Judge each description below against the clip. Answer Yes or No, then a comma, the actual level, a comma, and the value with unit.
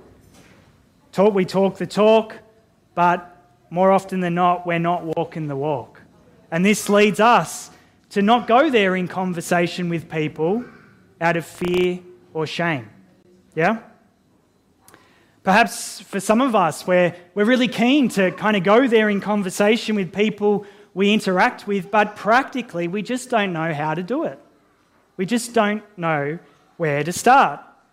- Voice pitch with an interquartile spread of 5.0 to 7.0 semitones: No, average, 3.9 semitones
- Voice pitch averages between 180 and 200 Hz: Yes, medium, 185 Hz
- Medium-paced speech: Yes, average, 155 wpm